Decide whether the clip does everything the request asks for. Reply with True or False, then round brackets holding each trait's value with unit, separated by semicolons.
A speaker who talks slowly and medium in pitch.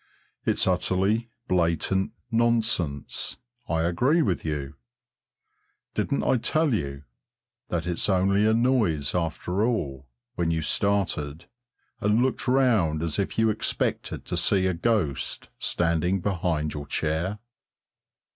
False (120 wpm; 90 Hz)